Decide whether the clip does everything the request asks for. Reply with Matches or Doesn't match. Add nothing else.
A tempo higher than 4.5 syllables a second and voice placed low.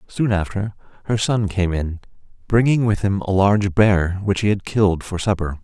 Matches